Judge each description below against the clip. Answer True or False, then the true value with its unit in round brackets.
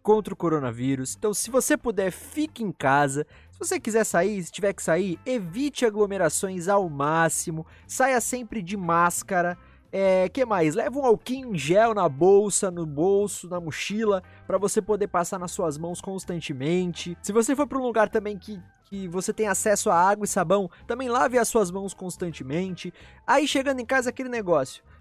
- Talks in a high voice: True (195 Hz)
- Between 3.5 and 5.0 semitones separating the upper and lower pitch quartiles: True (4.4 semitones)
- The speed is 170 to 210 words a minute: True (180 wpm)